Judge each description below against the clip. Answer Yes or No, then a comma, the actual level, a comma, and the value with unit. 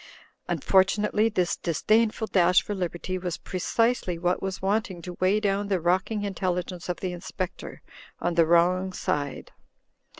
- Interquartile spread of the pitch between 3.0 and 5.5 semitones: No, narrow, 2.4 semitones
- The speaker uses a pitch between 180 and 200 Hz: Yes, medium, 185 Hz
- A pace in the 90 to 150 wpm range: Yes, average, 145 wpm